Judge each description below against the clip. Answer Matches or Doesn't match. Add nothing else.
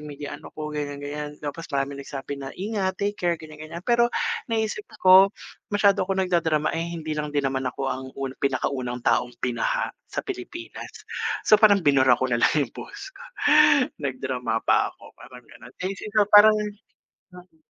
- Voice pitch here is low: Doesn't match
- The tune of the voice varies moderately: Doesn't match